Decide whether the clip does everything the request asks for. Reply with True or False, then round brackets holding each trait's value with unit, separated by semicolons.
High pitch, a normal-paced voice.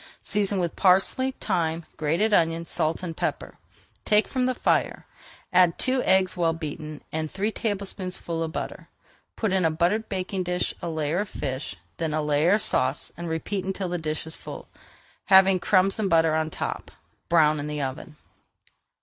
False (175 Hz; 175 wpm)